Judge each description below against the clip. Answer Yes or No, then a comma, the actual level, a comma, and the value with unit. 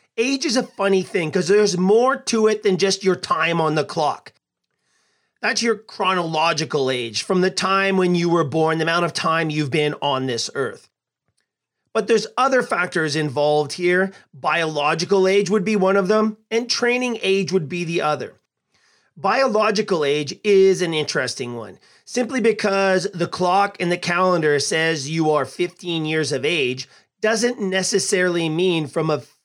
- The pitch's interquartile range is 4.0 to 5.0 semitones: Yes, average, 4.6 semitones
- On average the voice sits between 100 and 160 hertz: No, medium, 185 Hz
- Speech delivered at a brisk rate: No, average, 165 wpm